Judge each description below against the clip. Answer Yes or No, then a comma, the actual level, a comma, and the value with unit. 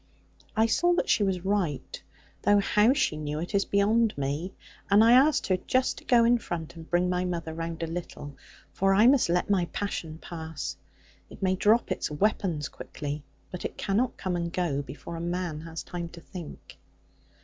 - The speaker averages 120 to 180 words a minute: No, average, 195 wpm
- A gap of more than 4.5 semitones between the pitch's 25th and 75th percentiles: No, average, 4.1 semitones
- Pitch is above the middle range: No, medium, 180 Hz